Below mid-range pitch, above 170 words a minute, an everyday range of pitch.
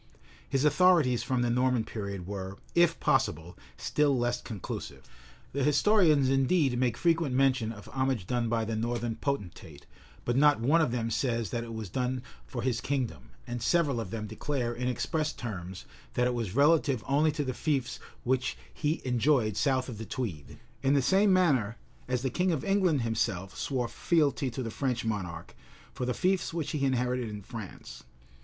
Yes: low, 125 Hz; average, 180 wpm; average, 3.9 semitones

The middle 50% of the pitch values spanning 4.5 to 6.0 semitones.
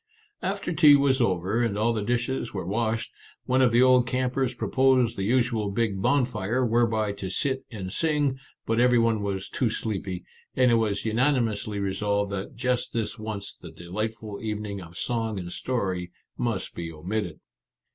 No: average, 3.9 semitones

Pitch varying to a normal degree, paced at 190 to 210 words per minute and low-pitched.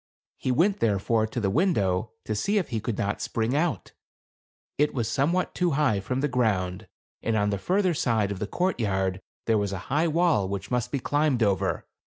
No: wide, 6.8 semitones; average, 195 wpm; low, 115 Hz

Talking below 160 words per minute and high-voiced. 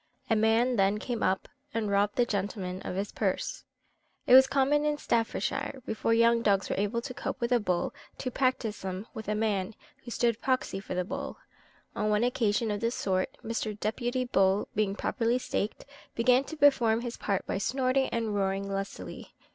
No: average, 185 wpm; high, 225 Hz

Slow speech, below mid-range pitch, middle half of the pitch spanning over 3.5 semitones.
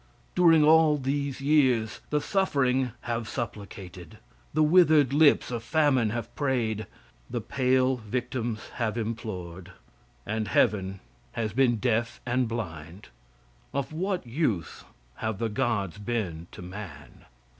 Yes: slow, 125 wpm; low, 120 Hz; average, 4.7 semitones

